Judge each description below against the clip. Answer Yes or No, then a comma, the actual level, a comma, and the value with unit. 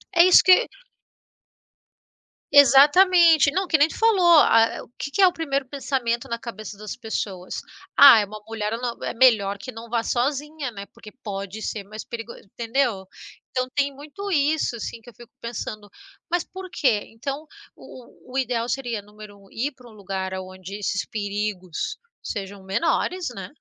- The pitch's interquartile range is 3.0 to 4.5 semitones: No, wide, 5.4 semitones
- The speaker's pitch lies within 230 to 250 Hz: Yes, high, 235 Hz